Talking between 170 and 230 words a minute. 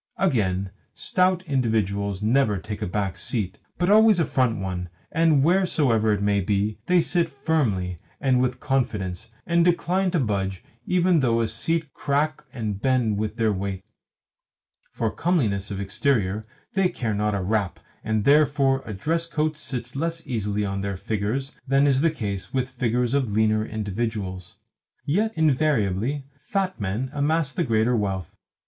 No: average, 155 wpm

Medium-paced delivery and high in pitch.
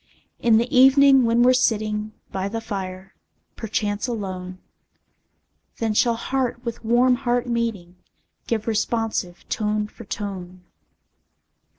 No: slow, 115 wpm; high, 225 Hz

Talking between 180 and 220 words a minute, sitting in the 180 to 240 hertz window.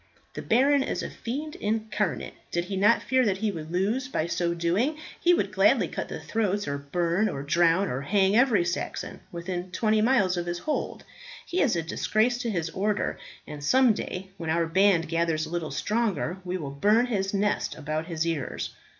Yes: average, 195 wpm; high, 190 Hz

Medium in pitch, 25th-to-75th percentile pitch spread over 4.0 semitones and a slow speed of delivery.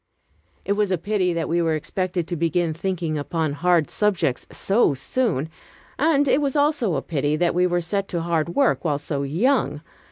No: medium, 175 Hz; average, 4.5 semitones; average, 190 wpm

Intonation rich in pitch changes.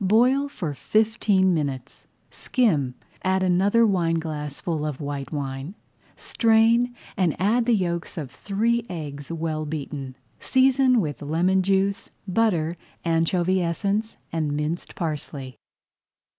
Yes: wide, 6.0 semitones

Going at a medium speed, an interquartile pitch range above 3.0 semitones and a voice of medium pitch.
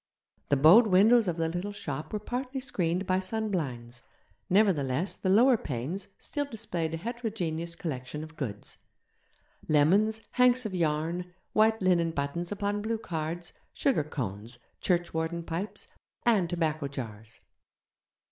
No: slow, 130 wpm; wide, 5.4 semitones; medium, 175 Hz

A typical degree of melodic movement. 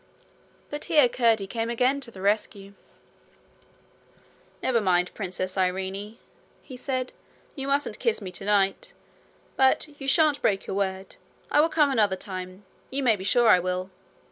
No: wide, 5.7 semitones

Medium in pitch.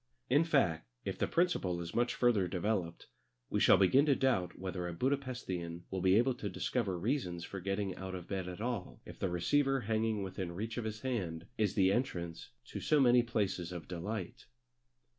No: low, 100 Hz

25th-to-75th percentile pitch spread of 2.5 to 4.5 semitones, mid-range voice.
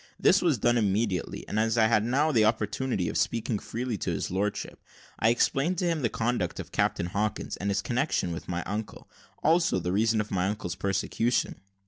No: average, 3.5 semitones; low, 110 Hz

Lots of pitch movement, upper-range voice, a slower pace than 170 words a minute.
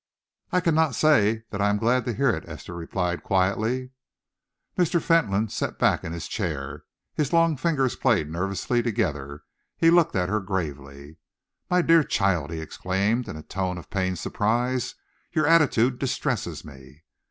No: wide, 7.2 semitones; low, 105 Hz; average, 160 wpm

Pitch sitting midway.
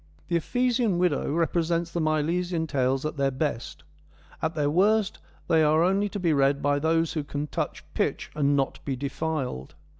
Yes: medium, 160 Hz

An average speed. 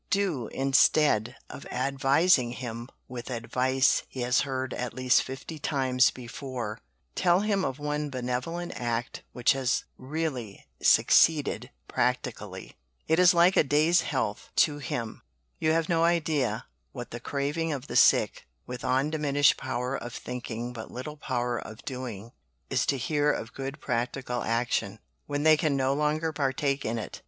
Yes: average, 150 wpm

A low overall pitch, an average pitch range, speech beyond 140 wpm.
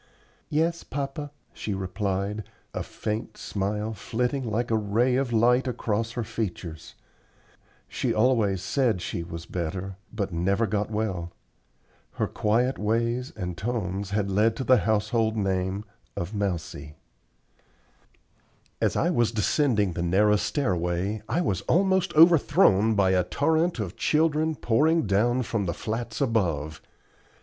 No: low, 110 Hz; average, 4.2 semitones; slow, 135 wpm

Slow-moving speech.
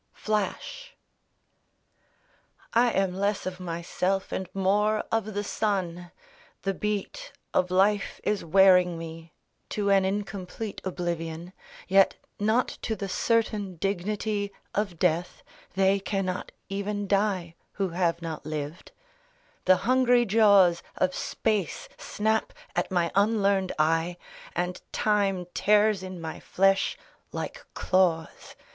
Yes: slow, 115 wpm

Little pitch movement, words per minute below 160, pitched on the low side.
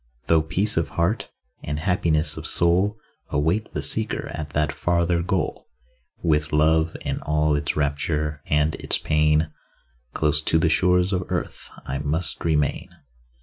Yes: narrow, 2.2 semitones; average, 145 wpm; very low, 80 Hz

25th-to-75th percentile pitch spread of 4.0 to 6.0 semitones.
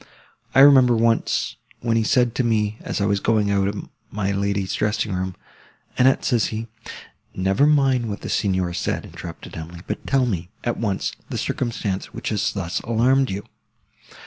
No: average, 3.6 semitones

